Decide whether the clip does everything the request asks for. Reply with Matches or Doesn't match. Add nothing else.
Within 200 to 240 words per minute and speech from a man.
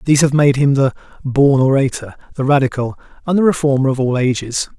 Doesn't match